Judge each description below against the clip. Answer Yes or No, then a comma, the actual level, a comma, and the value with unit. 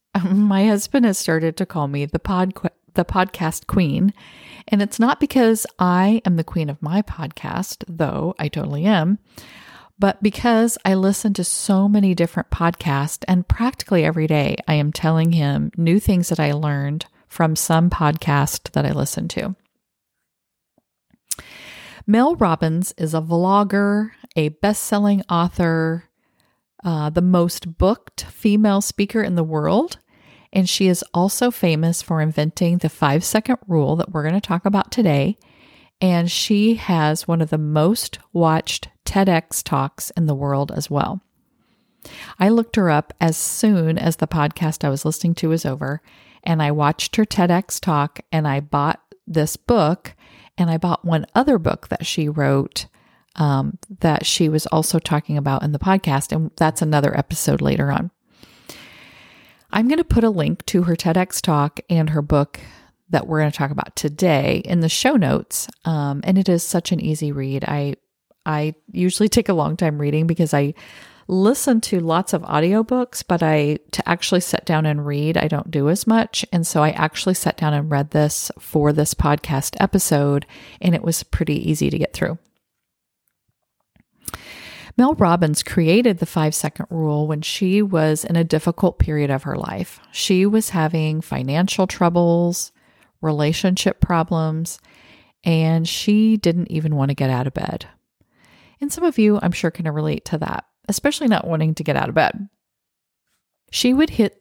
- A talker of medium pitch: Yes, medium, 170 Hz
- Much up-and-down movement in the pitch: No, average, 4.2 semitones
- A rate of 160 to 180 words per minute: Yes, average, 170 wpm